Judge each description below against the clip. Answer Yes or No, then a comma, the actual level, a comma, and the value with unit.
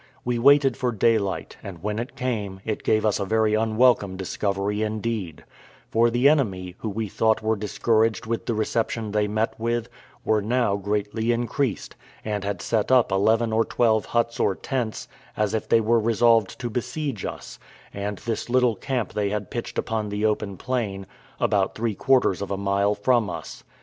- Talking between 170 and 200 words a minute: Yes, average, 180 wpm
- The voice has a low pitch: Yes, low, 110 Hz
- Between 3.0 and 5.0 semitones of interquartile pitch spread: No, narrow, 2.5 semitones